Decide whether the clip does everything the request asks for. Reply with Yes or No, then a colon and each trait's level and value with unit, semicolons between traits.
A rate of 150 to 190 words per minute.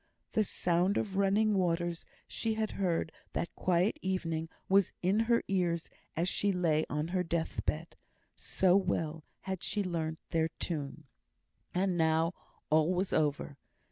No: average, 140 wpm